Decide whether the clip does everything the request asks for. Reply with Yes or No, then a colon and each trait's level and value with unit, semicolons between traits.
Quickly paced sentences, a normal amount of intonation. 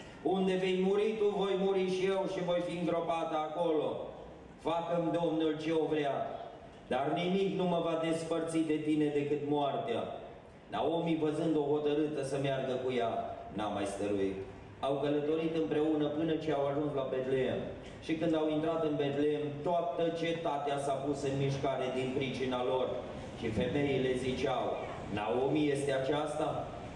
No: average, 155 wpm; average, 3.3 semitones